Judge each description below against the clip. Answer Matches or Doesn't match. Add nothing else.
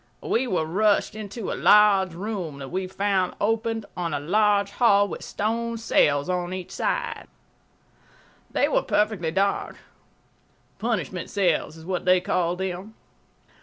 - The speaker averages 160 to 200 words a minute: Doesn't match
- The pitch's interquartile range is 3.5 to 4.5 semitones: Doesn't match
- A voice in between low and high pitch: Doesn't match